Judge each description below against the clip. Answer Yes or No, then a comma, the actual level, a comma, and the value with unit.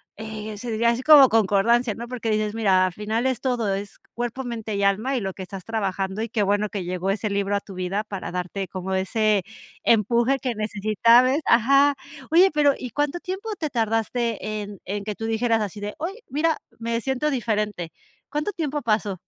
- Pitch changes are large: No, average, 3.7 semitones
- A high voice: Yes, high, 220 Hz